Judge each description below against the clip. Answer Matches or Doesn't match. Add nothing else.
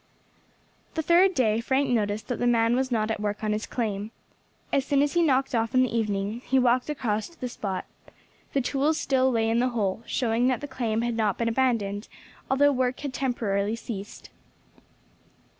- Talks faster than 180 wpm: Matches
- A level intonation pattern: Doesn't match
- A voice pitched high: Matches